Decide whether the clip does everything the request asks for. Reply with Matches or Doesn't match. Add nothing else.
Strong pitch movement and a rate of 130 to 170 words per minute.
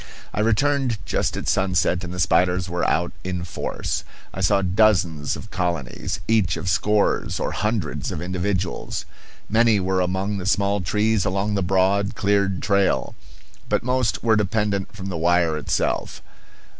Doesn't match